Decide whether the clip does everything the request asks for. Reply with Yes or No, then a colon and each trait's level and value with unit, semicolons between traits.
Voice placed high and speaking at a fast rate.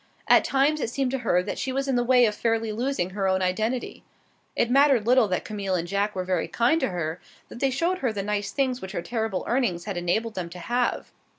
Yes: high, 220 Hz; fast, 240 wpm